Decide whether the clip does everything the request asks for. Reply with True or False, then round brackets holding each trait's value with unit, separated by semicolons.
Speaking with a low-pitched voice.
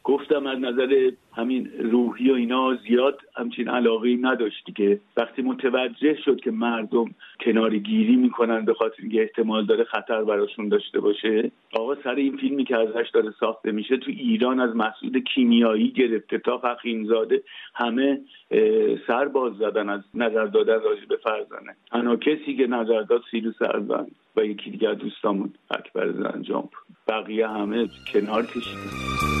True (125 Hz)